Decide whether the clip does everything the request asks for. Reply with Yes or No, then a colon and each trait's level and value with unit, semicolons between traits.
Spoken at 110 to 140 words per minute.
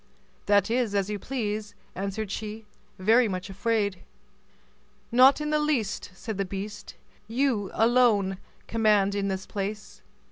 Yes: slow, 135 wpm